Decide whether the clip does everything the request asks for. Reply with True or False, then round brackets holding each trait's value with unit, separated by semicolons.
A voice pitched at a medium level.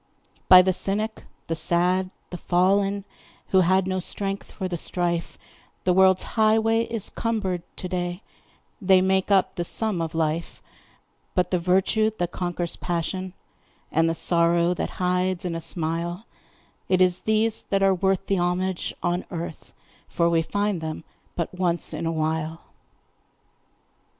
True (180 Hz)